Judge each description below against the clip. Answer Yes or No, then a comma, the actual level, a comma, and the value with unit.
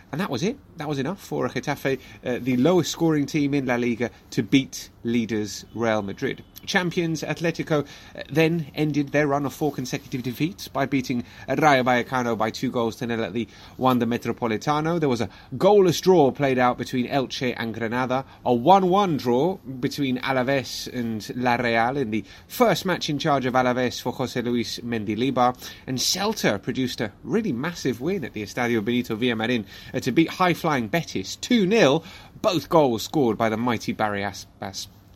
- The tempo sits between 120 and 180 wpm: Yes, average, 175 wpm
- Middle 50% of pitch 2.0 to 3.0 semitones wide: No, average, 4.1 semitones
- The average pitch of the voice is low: Yes, low, 125 Hz